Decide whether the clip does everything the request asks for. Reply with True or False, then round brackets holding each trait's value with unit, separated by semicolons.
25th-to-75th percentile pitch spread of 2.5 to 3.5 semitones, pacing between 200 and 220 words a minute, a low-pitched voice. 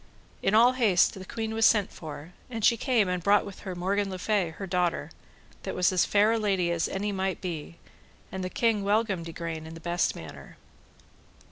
False (3.2 semitones; 205 wpm; 190 Hz)